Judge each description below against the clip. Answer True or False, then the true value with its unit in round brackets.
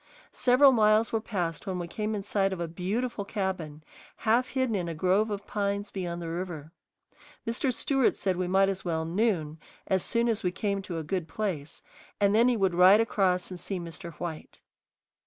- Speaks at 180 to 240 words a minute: True (195 wpm)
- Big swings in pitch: False (3.9 semitones)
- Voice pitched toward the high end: True (195 Hz)